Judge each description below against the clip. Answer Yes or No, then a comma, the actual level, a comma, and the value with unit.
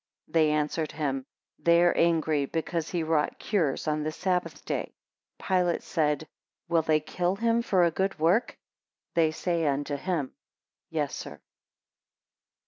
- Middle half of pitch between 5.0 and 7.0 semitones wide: No, narrow, 2.5 semitones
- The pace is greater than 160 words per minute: No, average, 145 wpm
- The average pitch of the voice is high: No, medium, 160 Hz